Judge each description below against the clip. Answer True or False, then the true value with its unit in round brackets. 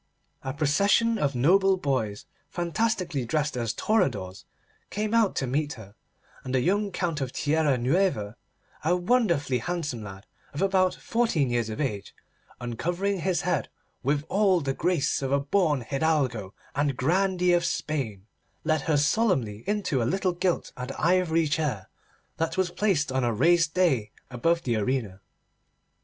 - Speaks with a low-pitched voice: False (155 Hz)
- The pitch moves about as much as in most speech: False (6.2 semitones)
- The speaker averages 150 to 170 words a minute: True (155 wpm)